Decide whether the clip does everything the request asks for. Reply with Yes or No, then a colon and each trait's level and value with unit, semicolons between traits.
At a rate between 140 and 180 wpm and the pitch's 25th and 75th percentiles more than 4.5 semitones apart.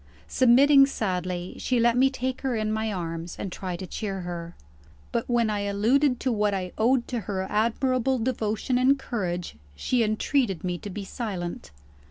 Yes: average, 175 wpm; average, 5.1 semitones